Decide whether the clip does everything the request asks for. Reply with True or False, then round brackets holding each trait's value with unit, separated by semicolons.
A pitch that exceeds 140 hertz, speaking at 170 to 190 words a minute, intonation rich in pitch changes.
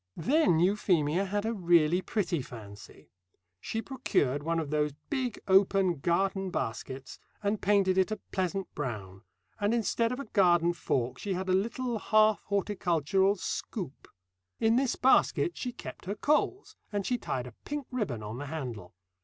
False (190 Hz; 160 wpm; 6.3 semitones)